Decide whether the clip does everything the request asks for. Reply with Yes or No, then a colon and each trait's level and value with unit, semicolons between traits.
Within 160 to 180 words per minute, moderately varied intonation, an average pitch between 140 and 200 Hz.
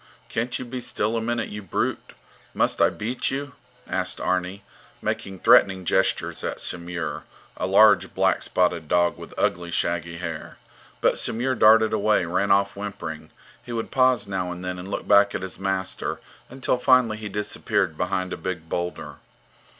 No: average, 165 wpm; average, 3.7 semitones; low, 100 Hz